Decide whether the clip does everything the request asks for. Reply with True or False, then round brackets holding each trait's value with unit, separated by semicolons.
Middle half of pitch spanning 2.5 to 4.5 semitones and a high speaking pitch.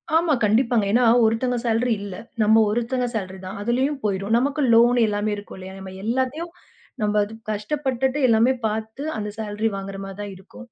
True (3.4 semitones; 220 Hz)